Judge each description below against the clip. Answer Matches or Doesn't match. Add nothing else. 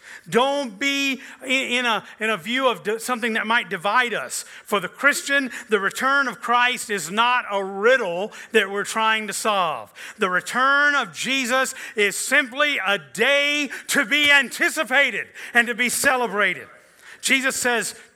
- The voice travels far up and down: Doesn't match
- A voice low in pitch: Doesn't match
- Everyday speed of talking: Matches